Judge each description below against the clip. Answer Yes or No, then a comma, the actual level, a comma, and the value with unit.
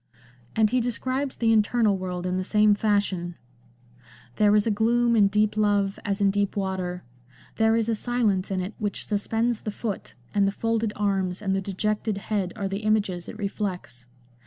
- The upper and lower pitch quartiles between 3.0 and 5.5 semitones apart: No, narrow, 2.6 semitones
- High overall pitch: Yes, high, 205 Hz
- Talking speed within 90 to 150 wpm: No, average, 190 wpm